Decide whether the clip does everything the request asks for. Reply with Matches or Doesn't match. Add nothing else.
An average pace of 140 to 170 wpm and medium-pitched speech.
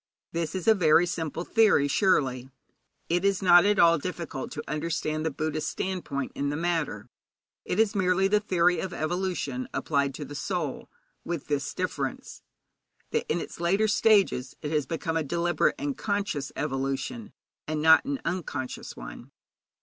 Matches